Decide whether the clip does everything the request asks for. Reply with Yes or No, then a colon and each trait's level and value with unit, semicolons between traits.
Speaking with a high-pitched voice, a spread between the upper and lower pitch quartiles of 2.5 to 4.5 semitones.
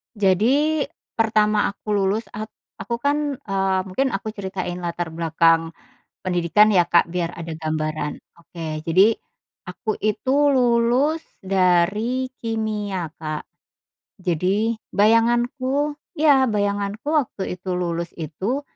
No: high, 200 Hz; average, 5.1 semitones